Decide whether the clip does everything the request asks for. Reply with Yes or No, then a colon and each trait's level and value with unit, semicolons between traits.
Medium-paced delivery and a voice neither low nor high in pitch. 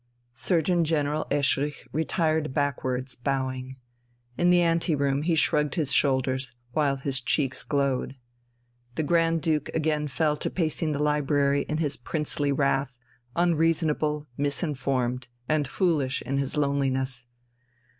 No: slow, 125 wpm; medium, 145 Hz